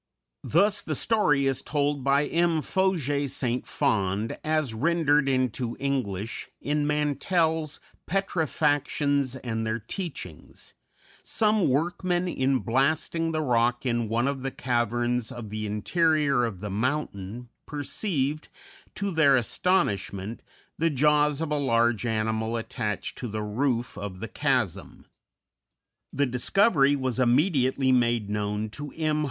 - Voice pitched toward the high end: No, low, 135 Hz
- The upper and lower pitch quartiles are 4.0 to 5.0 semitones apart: Yes, average, 4.6 semitones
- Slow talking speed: Yes, slow, 125 wpm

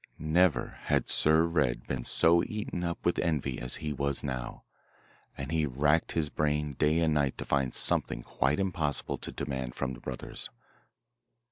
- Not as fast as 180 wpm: Yes, average, 165 wpm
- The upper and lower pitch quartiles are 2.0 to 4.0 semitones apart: Yes, average, 3.3 semitones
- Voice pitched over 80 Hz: No, very low, 75 Hz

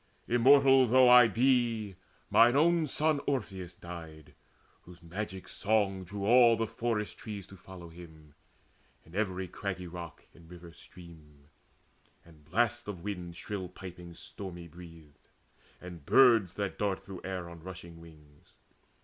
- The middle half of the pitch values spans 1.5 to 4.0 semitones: No, average, 4.8 semitones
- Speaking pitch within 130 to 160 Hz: No, very low, 95 Hz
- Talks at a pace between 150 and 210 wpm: No, average, 140 wpm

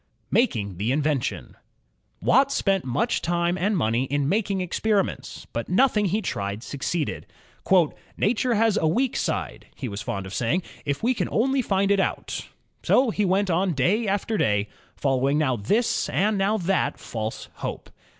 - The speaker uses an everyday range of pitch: No, wide, 8.2 semitones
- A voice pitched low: No, medium, 180 Hz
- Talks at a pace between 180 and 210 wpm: No, average, 165 wpm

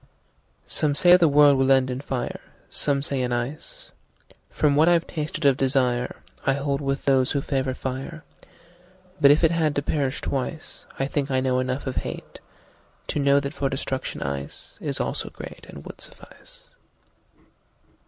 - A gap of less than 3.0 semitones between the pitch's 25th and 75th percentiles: Yes, narrow, 2.4 semitones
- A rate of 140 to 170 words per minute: Yes, average, 145 wpm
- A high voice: No, medium, 140 Hz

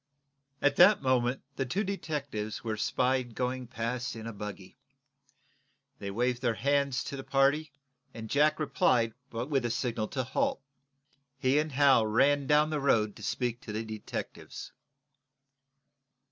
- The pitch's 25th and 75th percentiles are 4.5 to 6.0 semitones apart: No, average, 3.6 semitones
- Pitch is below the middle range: Yes, low, 125 Hz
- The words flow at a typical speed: Yes, average, 145 wpm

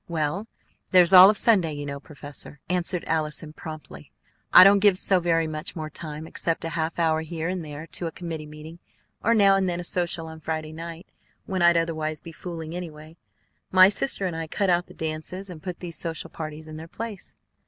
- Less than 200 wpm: No, fast, 205 wpm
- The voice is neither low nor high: Yes, medium, 165 Hz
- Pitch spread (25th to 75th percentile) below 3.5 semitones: Yes, narrow, 2.5 semitones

